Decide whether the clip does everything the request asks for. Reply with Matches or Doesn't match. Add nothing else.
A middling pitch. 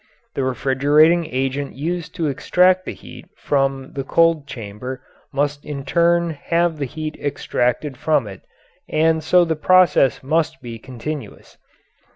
Matches